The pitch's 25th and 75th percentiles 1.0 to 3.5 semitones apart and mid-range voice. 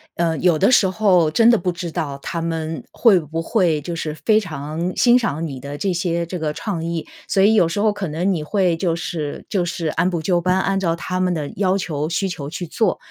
Yes: average, 3.0 semitones; medium, 170 Hz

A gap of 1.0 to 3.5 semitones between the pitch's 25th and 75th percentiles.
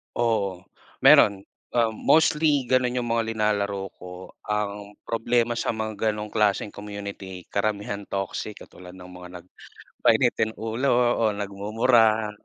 Yes: narrow, 2.4 semitones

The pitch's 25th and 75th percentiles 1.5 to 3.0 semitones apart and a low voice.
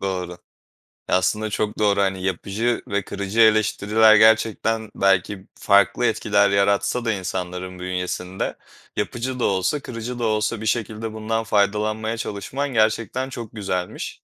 Yes: narrow, 2.4 semitones; low, 105 Hz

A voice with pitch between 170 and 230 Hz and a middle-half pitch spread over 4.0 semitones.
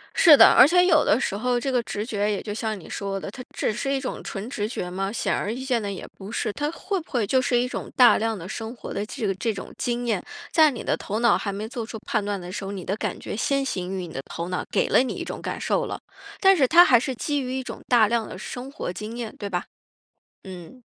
Yes: high, 225 Hz; average, 4.5 semitones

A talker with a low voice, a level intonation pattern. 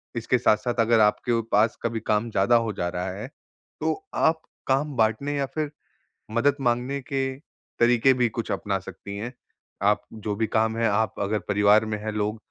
No: low, 115 Hz; average, 3.1 semitones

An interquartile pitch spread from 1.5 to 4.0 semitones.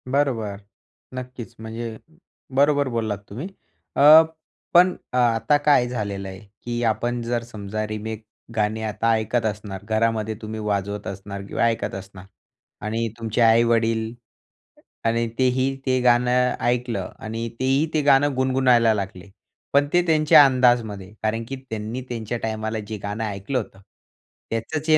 Yes: average, 2.8 semitones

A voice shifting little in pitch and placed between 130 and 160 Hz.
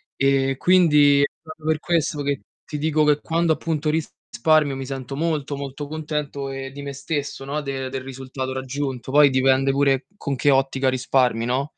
Yes: narrow, 2.0 semitones; medium, 140 Hz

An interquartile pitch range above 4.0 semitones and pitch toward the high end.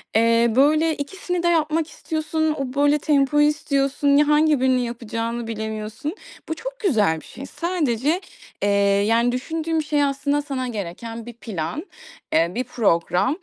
Yes: average, 4.9 semitones; very high, 275 Hz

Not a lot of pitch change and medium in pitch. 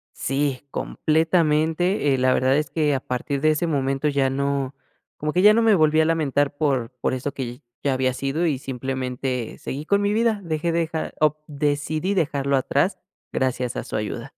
No: average, 3.2 semitones; medium, 145 Hz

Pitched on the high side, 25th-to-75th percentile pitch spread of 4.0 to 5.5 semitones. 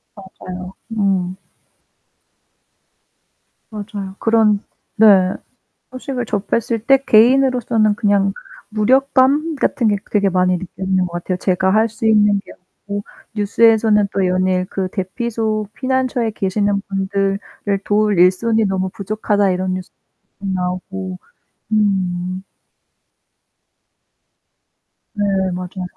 No: high, 200 Hz; average, 2.8 semitones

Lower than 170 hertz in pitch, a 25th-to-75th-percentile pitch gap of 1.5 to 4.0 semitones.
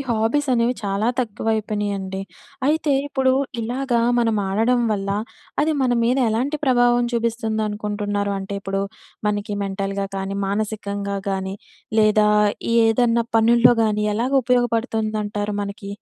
No: high, 220 Hz; average, 2.9 semitones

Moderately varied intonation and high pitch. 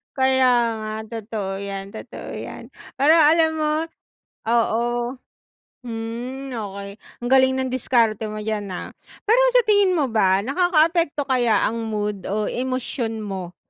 Yes: average, 4.2 semitones; high, 235 Hz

